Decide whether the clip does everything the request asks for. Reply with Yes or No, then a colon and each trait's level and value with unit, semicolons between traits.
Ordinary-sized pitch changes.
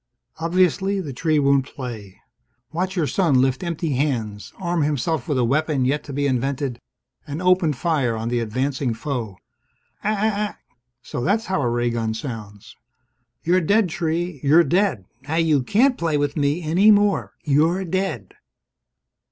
No: wide, 5.7 semitones